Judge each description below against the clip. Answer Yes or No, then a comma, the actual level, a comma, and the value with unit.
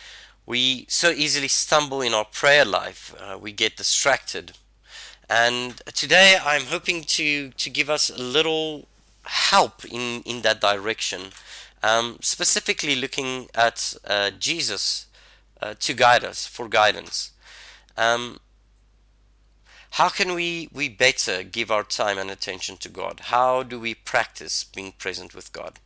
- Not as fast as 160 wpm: Yes, average, 140 wpm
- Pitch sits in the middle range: No, low, 125 Hz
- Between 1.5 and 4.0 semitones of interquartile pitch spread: No, average, 5.3 semitones